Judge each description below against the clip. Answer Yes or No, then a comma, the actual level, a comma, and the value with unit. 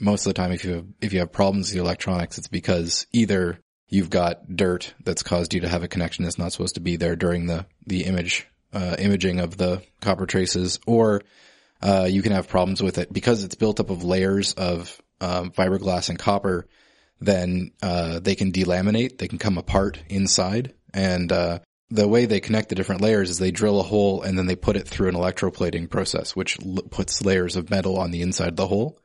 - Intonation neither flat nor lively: No, narrow, 1.9 semitones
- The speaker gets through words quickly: Yes, fast, 220 wpm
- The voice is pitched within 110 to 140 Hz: No, very low, 95 Hz